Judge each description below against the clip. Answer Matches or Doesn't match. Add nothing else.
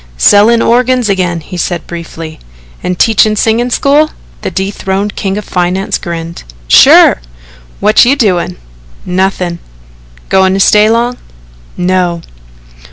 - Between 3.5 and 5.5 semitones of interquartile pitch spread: Matches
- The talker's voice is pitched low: Doesn't match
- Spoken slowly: Matches